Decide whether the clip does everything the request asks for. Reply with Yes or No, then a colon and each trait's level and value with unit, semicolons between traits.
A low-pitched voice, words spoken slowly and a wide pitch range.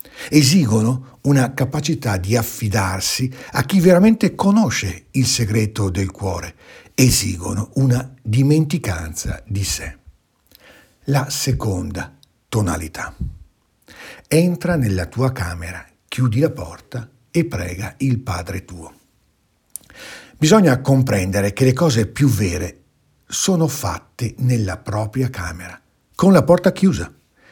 Yes: low, 120 Hz; slow, 105 wpm; wide, 6.3 semitones